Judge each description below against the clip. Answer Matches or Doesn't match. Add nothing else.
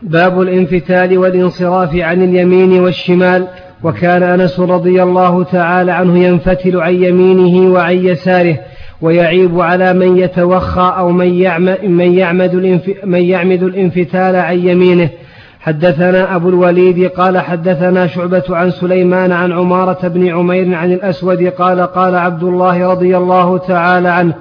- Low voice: Doesn't match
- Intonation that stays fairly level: Matches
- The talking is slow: Doesn't match